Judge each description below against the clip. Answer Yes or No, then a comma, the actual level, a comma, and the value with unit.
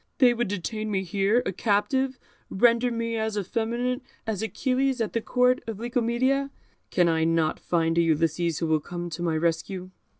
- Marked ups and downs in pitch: Yes, wide, 5.9 semitones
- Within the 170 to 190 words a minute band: Yes, average, 175 wpm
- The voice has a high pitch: Yes, high, 215 Hz